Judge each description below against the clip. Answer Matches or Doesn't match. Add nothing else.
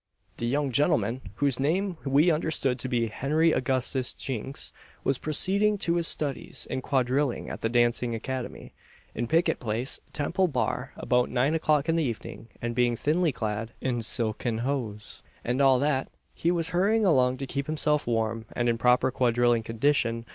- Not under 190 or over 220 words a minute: Doesn't match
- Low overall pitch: Matches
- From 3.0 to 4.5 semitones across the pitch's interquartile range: Matches